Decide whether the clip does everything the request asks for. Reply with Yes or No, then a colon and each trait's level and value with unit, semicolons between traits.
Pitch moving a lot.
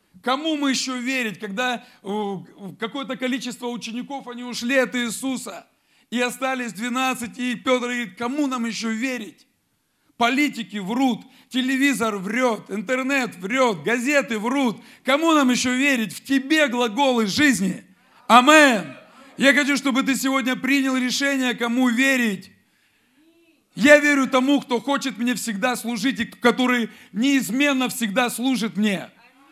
No: narrow, 2.5 semitones